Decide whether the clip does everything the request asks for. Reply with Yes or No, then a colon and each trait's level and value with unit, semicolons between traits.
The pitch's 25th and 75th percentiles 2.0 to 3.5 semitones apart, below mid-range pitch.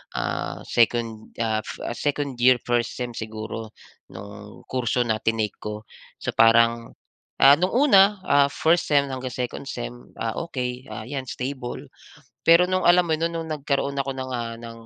No: average, 3.9 semitones; low, 125 Hz